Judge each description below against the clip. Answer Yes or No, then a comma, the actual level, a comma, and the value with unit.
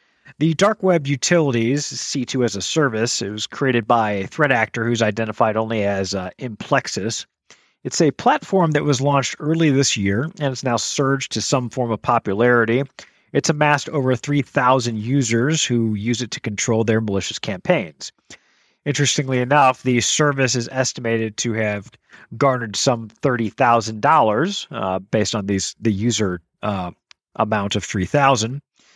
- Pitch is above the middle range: No, low, 120 Hz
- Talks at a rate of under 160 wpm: Yes, average, 150 wpm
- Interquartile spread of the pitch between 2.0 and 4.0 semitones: No, average, 4.4 semitones